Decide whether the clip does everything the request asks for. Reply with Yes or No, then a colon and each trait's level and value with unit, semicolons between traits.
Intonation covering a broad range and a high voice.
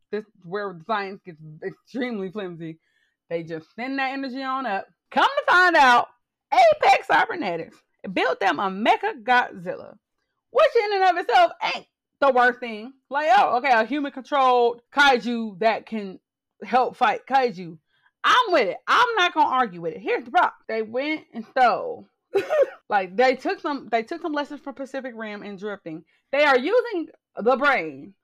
Yes: wide, 6.8 semitones; very high, 255 Hz